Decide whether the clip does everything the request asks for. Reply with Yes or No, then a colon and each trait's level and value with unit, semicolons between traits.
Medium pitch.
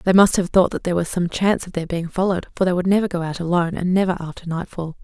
Yes: medium, 180 Hz